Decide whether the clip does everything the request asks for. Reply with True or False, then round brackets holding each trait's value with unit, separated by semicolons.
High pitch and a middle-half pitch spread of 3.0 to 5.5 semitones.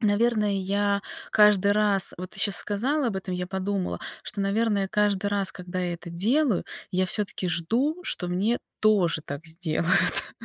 False (200 Hz; 2.6 semitones)